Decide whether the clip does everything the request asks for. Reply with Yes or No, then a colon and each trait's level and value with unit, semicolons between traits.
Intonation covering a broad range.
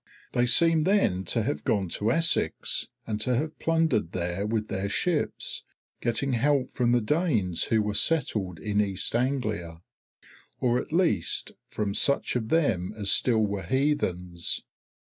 Yes: wide, 6.2 semitones